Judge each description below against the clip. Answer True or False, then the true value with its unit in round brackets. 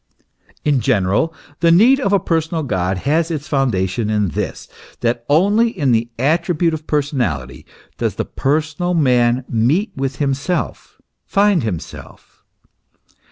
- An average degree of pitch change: False (6.0 semitones)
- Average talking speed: False (130 wpm)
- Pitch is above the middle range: False (140 Hz)